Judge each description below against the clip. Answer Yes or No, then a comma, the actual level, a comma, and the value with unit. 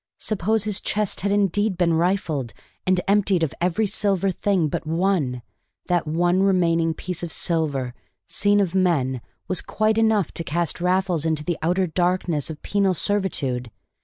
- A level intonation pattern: No, average, 3.5 semitones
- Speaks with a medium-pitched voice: Yes, medium, 180 Hz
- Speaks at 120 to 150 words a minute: No, average, 160 wpm